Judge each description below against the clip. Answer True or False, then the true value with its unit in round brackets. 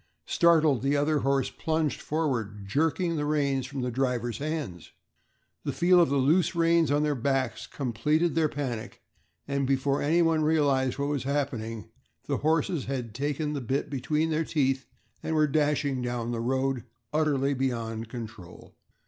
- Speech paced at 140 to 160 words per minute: True (155 wpm)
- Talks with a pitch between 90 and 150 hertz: True (140 Hz)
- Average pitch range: True (3.3 semitones)